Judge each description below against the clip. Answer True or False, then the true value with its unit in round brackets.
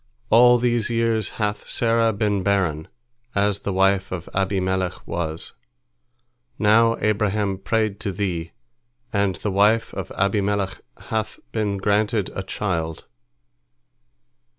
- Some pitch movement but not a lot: False (2.3 semitones)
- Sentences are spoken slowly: True (115 wpm)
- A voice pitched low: True (100 Hz)